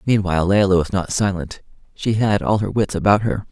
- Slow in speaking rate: No, fast, 205 wpm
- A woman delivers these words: No, male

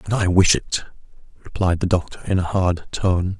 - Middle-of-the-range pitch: No, very low, 90 Hz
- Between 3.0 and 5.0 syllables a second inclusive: Yes, 4.8 syllables/s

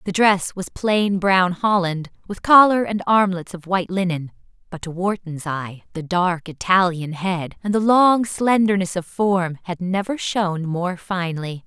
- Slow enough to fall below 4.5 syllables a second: Yes, 4.2 syllables/s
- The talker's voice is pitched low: No, medium, 185 Hz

